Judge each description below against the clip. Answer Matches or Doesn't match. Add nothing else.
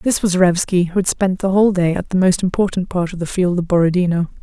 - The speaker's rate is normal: Doesn't match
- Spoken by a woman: Matches